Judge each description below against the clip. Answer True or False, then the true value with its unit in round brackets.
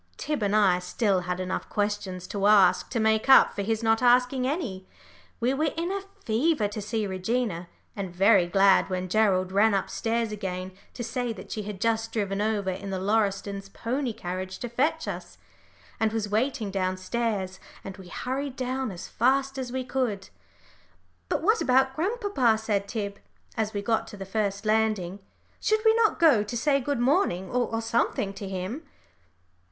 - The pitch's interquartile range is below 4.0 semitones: False (4.4 semitones)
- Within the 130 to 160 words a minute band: False (180 wpm)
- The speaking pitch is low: False (220 Hz)